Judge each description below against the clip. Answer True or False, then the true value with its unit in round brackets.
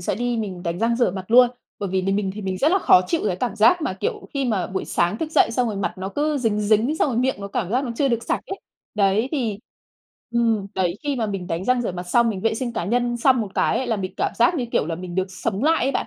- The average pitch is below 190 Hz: False (225 Hz)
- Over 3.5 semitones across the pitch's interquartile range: True (4.5 semitones)